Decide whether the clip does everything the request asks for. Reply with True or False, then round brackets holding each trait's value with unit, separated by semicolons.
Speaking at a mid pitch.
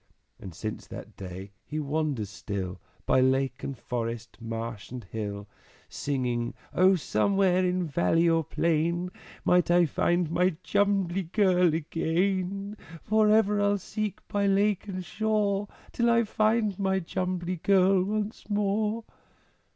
True (180 Hz)